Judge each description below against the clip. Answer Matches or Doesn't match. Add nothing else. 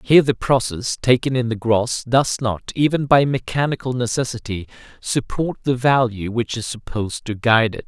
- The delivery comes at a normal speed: Matches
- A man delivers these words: Matches